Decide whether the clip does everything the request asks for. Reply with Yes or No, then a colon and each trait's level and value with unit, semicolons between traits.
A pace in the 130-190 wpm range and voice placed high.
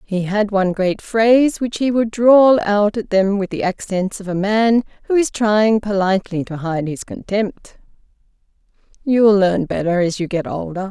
Yes: average, 180 wpm; high, 205 Hz